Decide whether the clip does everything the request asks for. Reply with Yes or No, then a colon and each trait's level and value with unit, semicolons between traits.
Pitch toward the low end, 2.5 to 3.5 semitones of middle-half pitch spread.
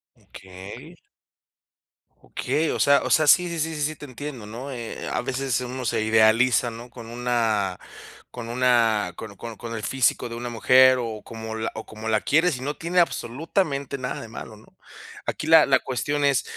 No: low, 125 Hz; average, 4.0 semitones